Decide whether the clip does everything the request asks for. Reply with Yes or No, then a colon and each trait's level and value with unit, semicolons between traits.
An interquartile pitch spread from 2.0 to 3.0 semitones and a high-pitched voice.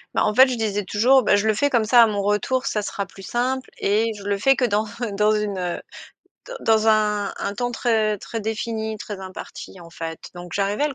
Yes: narrow, 2.6 semitones; high, 215 Hz